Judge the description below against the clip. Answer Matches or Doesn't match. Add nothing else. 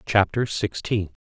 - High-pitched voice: Doesn't match